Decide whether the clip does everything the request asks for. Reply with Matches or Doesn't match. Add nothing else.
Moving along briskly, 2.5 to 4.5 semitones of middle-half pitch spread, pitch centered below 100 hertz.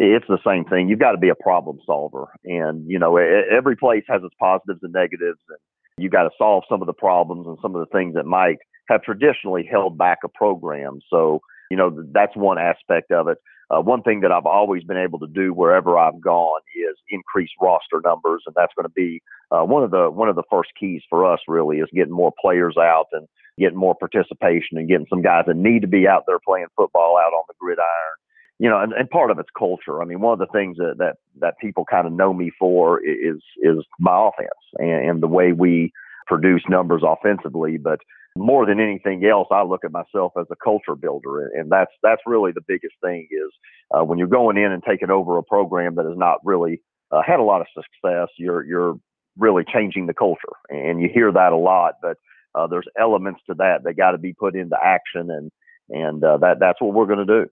Matches